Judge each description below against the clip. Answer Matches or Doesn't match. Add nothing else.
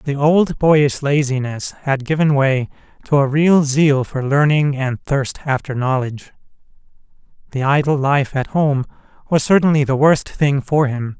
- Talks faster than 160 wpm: Doesn't match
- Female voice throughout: Doesn't match